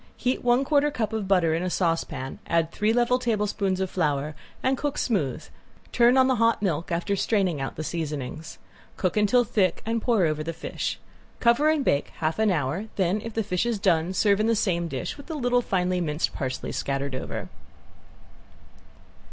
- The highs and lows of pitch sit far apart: Yes, wide, 6.1 semitones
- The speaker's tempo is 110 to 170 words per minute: No, average, 185 wpm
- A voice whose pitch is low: No, high, 190 Hz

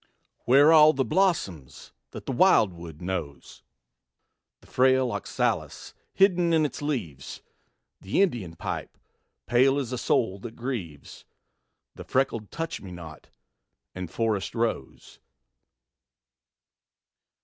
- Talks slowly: Yes, slow, 110 wpm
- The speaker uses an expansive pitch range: Yes, wide, 7.7 semitones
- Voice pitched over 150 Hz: No, low, 120 Hz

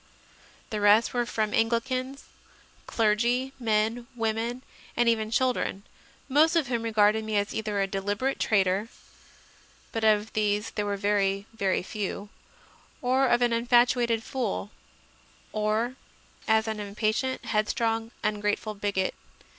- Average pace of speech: No, slow, 130 wpm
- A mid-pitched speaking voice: No, high, 220 Hz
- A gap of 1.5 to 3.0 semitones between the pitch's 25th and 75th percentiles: Yes, narrow, 2.5 semitones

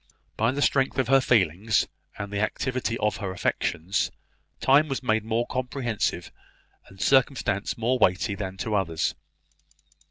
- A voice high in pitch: No, low, 110 Hz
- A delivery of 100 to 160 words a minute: Yes, average, 145 wpm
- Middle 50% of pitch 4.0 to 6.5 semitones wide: Yes, average, 4.6 semitones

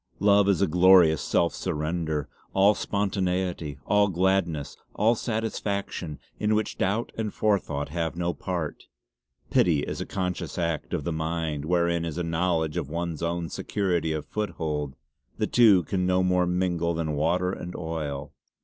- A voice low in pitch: Yes, very low, 85 Hz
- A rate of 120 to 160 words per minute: Yes, average, 155 wpm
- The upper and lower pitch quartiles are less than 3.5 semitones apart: Yes, average, 3.0 semitones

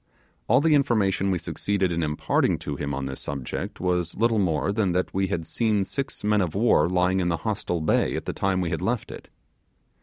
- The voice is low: Yes, very low, 95 Hz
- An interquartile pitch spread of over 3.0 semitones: Yes, average, 3.8 semitones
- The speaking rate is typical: No, fast, 215 wpm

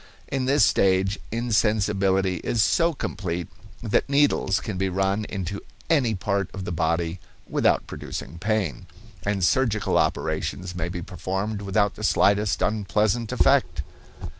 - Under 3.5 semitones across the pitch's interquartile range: Yes, average, 2.7 semitones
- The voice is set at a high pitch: No, low, 100 Hz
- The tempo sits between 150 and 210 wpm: No, slow, 135 wpm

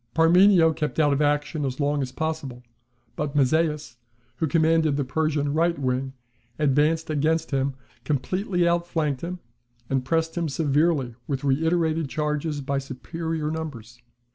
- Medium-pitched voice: Yes, medium, 150 Hz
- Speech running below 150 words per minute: Yes, average, 140 wpm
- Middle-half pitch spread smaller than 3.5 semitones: Yes, average, 2.8 semitones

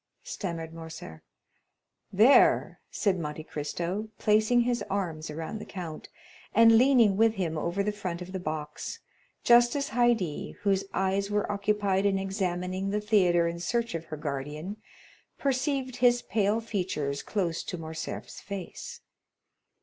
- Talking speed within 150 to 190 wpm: No, average, 140 wpm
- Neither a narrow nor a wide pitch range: Yes, average, 4.7 semitones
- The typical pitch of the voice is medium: No, high, 195 Hz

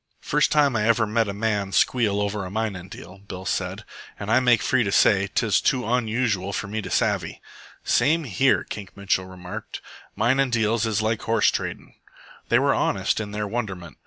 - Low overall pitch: Yes, low, 110 Hz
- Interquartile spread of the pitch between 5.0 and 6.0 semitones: No, average, 2.9 semitones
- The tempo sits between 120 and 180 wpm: No, average, 190 wpm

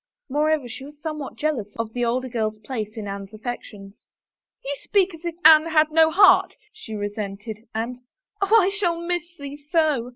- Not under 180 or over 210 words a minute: Yes, average, 190 wpm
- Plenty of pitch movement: Yes, wide, 6.6 semitones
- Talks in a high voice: Yes, very high, 275 Hz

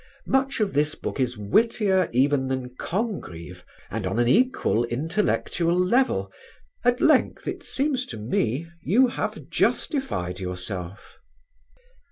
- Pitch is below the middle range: No, medium, 150 Hz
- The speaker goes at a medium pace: No, slow, 125 wpm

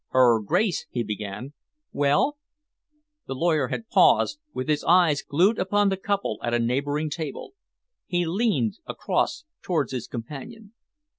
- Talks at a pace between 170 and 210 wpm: No, average, 140 wpm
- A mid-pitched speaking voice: Yes, medium, 155 Hz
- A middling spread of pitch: No, wide, 7.5 semitones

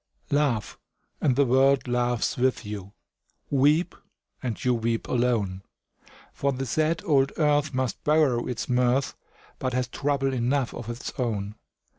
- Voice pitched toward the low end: Yes, low, 130 Hz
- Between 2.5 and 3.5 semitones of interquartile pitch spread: Yes, average, 2.8 semitones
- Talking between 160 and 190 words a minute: No, average, 140 wpm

